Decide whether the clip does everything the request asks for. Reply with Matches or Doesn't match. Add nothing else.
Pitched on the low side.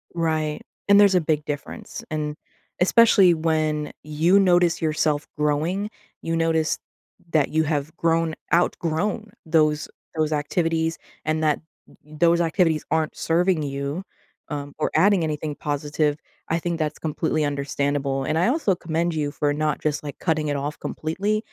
Doesn't match